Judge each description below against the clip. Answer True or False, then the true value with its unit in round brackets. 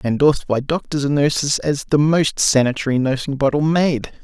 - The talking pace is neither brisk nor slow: True (170 wpm)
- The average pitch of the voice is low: False (145 Hz)